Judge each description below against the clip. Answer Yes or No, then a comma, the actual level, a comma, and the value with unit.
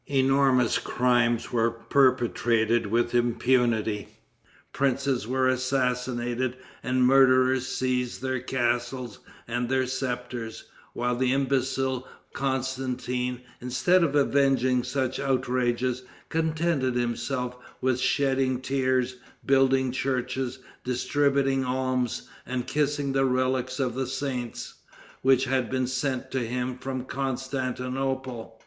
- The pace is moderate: No, slow, 105 wpm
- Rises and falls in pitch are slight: Yes, narrow, 1.4 semitones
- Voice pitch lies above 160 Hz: No, low, 130 Hz